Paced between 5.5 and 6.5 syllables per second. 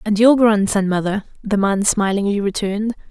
No: 5.2 syllables/s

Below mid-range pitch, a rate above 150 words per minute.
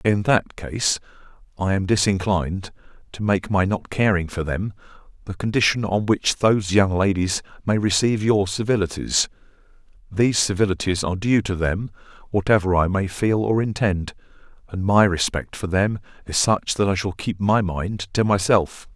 Yes: low, 100 Hz; average, 160 wpm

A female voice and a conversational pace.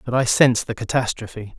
No: male; average, 190 wpm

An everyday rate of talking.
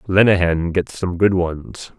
Yes: average, 150 wpm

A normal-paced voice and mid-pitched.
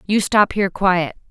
No: average, 185 wpm; high, 195 Hz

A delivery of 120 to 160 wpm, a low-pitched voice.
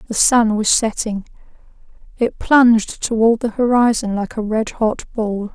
No: average, 140 wpm; high, 225 Hz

